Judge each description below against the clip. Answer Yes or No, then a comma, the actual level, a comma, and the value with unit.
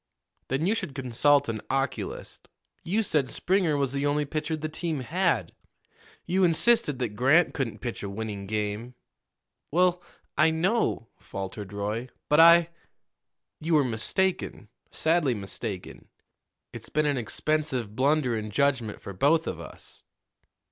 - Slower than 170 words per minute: Yes, average, 140 wpm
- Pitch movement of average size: No, wide, 6.3 semitones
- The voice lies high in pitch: No, medium, 140 Hz